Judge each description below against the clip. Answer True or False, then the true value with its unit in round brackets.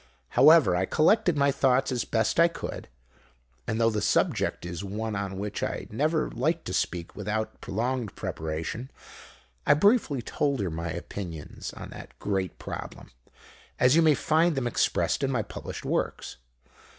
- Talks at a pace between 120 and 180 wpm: True (160 wpm)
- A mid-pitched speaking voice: False (115 Hz)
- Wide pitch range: True (7.0 semitones)